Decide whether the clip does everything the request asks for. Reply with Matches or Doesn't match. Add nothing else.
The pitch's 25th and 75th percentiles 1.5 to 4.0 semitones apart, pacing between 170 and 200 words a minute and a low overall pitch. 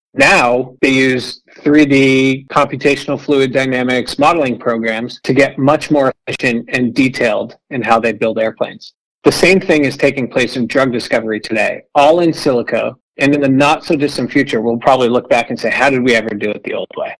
Matches